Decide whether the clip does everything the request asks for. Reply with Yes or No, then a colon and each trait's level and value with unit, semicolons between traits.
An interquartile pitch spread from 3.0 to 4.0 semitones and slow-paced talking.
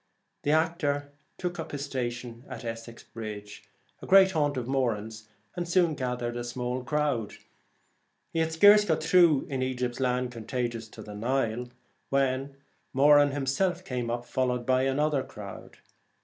No: average, 3.7 semitones; average, 155 wpm